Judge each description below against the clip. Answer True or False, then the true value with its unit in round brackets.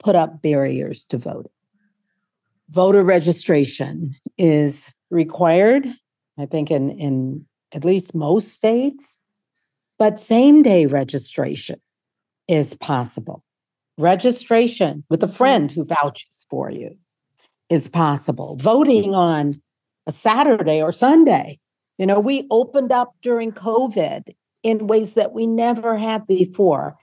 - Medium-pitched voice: True (180 Hz)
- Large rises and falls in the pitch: True (6.9 semitones)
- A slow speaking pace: True (115 wpm)